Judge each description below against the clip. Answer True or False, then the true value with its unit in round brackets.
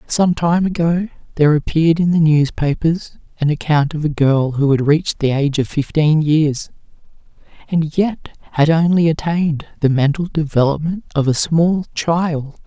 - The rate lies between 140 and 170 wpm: True (155 wpm)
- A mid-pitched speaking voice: True (155 Hz)